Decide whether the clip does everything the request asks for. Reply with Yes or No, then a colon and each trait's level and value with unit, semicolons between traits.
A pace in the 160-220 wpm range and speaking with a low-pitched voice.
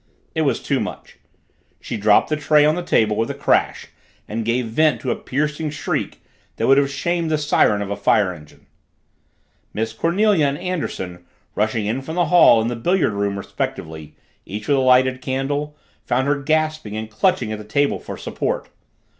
Yes: average, 190 wpm; low, 130 Hz